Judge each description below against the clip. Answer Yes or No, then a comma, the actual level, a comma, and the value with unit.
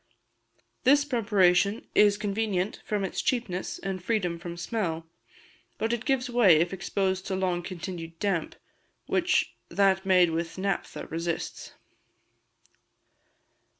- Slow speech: Yes, slow, 115 wpm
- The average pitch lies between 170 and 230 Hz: Yes, high, 190 Hz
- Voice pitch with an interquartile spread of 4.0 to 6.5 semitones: No, average, 3.3 semitones